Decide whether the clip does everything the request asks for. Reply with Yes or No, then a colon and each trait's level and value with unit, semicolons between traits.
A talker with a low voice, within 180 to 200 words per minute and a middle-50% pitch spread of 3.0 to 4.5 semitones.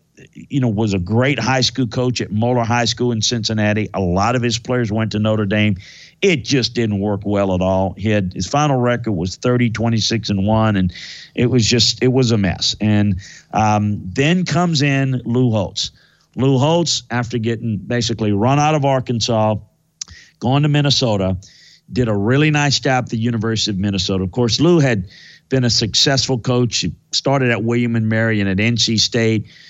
Yes: low, 115 Hz; average, 190 wpm; average, 3.3 semitones